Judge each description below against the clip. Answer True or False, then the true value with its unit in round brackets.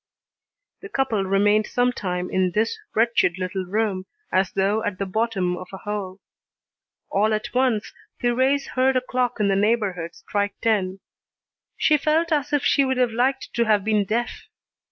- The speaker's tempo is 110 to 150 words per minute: False (170 wpm)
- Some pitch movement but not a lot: True (4.4 semitones)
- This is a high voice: True (215 Hz)